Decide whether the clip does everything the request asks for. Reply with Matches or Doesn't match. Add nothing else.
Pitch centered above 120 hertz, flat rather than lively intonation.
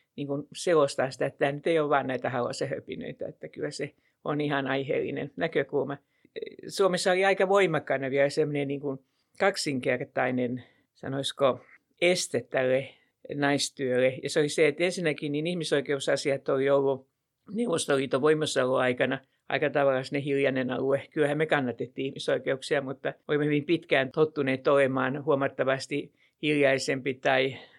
Matches